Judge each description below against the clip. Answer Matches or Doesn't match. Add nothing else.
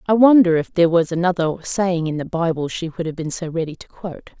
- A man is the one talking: Doesn't match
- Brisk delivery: Matches